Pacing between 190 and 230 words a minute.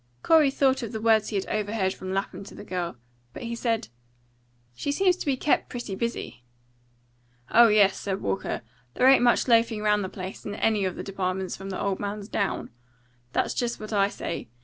Yes: average, 200 wpm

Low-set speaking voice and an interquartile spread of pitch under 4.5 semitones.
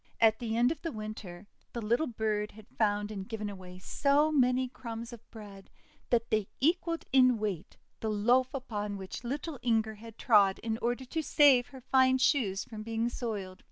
No: high, 230 Hz; average, 3.5 semitones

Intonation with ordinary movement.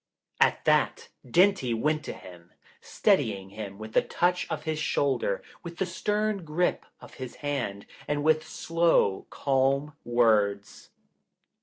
No: wide, 7.7 semitones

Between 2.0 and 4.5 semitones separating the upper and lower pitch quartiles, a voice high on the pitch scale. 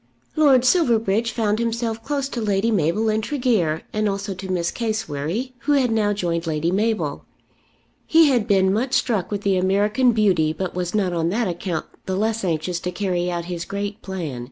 Yes: average, 4.2 semitones; high, 205 Hz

